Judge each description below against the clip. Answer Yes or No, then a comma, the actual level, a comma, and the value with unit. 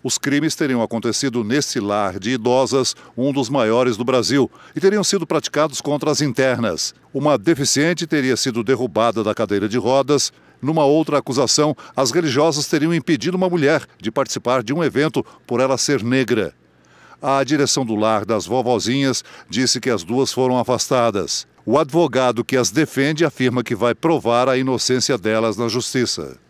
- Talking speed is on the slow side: No, average, 165 wpm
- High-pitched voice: No, low, 130 Hz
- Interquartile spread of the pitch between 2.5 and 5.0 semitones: Yes, average, 3.5 semitones